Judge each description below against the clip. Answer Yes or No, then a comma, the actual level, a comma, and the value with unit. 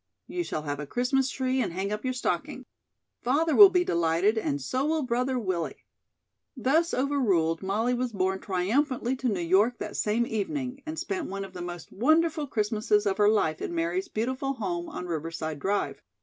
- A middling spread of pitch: No, wide, 6.3 semitones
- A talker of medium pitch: No, high, 225 Hz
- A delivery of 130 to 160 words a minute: No, average, 185 wpm